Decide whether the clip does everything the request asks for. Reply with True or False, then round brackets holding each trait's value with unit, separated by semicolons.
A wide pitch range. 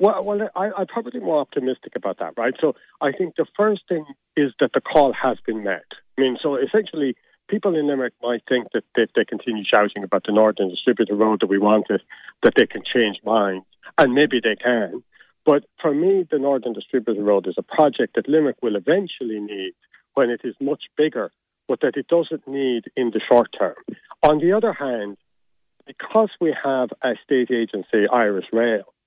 True (6.4 semitones)